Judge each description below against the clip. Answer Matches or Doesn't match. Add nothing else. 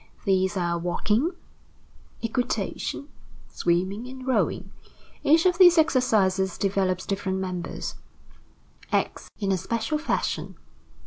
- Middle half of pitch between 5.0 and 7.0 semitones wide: Matches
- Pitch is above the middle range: Matches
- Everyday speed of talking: Doesn't match